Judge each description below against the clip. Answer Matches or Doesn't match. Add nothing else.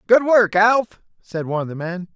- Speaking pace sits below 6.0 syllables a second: Matches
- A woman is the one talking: Doesn't match